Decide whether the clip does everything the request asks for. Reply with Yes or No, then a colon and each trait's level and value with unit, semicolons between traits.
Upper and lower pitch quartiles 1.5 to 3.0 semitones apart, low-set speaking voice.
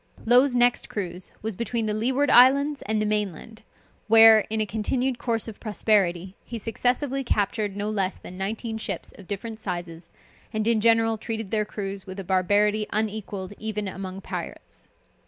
No: narrow, 2.6 semitones; high, 215 Hz